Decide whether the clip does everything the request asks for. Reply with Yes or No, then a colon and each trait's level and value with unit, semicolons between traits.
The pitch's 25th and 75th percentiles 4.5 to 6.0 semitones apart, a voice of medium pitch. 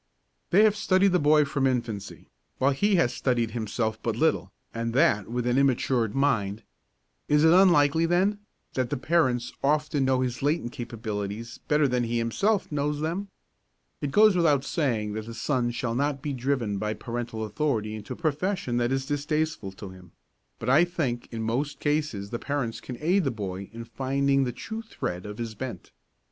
No: average, 4.8 semitones; low, 130 Hz